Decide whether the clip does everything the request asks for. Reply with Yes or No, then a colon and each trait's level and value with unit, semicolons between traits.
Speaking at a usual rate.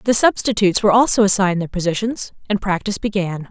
Yes: average, 170 wpm